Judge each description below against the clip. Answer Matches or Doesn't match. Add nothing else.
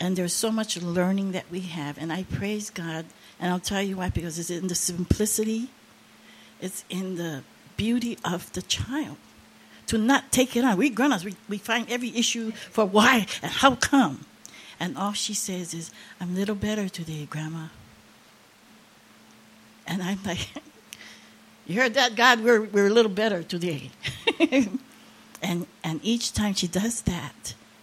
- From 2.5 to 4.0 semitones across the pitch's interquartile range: Doesn't match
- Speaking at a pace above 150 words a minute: Matches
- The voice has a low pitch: Doesn't match